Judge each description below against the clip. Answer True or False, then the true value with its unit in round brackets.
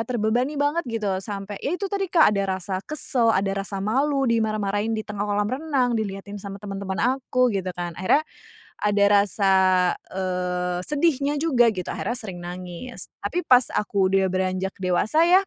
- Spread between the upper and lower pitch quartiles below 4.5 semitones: False (4.9 semitones)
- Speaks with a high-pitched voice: True (210 Hz)